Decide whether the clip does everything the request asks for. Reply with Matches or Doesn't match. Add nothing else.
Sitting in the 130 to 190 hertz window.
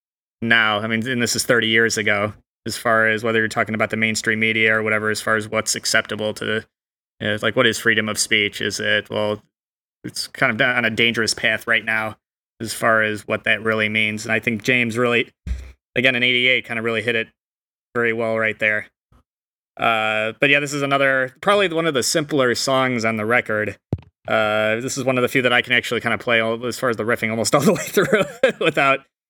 Doesn't match